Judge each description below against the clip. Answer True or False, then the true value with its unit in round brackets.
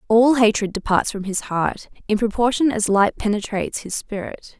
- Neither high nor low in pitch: False (215 Hz)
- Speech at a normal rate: True (170 wpm)